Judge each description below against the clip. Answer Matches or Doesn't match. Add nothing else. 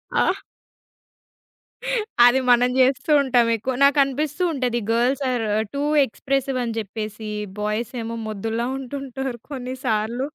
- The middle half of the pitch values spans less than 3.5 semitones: Matches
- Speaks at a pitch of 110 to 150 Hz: Doesn't match